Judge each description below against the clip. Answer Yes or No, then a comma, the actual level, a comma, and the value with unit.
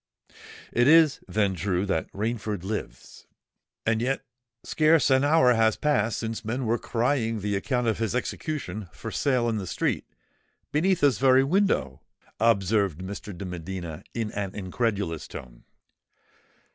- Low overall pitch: Yes, low, 110 Hz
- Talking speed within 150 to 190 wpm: No, average, 140 wpm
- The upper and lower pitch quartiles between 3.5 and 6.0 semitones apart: Yes, average, 4.7 semitones